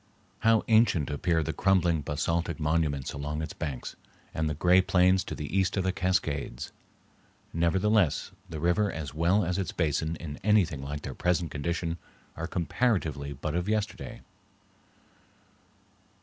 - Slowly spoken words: No, average, 145 wpm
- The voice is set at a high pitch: No, very low, 85 Hz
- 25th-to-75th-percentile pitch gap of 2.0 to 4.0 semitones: Yes, average, 3.7 semitones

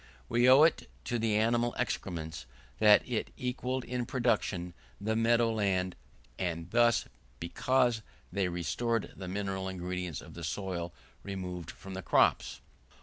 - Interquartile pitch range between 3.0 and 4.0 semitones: No, average, 4.8 semitones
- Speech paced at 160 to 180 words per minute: No, average, 140 wpm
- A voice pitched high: No, low, 100 Hz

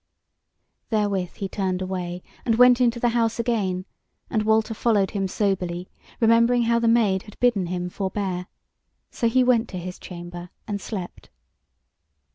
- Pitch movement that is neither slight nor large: Yes, average, 4.0 semitones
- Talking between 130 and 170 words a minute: Yes, average, 150 wpm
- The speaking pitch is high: Yes, high, 205 Hz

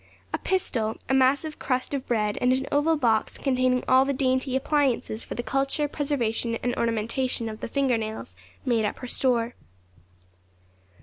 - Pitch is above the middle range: Yes, very high, 255 Hz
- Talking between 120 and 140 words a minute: No, average, 165 wpm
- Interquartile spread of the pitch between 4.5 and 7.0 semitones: No, average, 2.9 semitones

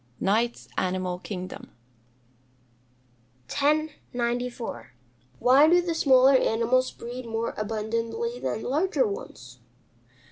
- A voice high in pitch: Yes, high, 240 Hz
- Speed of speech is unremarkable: No, slow, 95 wpm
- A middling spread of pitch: Yes, average, 4.6 semitones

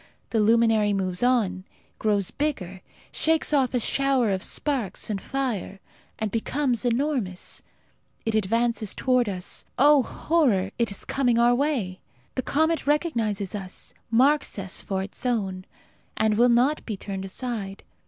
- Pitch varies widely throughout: No, average, 5.0 semitones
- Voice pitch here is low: No, high, 230 Hz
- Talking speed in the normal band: Yes, average, 145 wpm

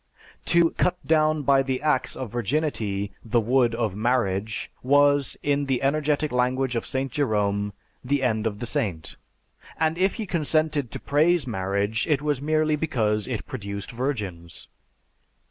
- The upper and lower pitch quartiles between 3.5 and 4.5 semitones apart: No, wide, 5.5 semitones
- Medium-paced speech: Yes, average, 150 wpm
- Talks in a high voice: No, low, 130 Hz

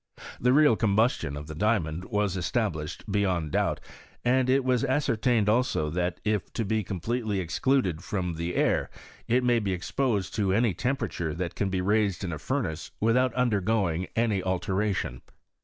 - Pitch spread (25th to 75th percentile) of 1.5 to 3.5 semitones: No, average, 5.1 semitones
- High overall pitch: No, low, 105 Hz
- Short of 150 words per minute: No, average, 165 wpm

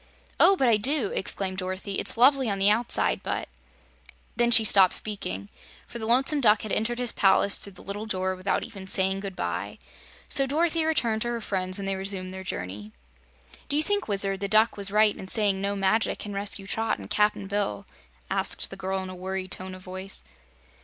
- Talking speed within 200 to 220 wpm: Yes, fast, 205 wpm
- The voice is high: Yes, high, 200 Hz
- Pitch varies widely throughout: No, average, 3.0 semitones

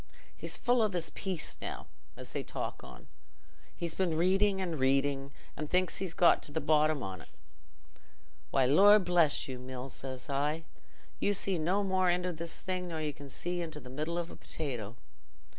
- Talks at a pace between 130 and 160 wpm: No, average, 180 wpm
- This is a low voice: No, medium, 160 Hz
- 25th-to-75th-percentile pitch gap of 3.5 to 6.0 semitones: Yes, average, 4.7 semitones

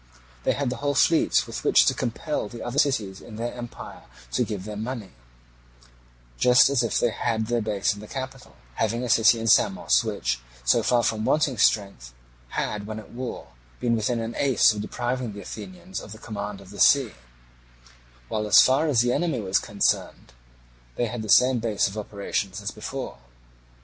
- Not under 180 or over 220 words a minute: Yes, average, 190 wpm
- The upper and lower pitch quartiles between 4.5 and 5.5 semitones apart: No, average, 3.2 semitones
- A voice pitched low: Yes, low, 115 Hz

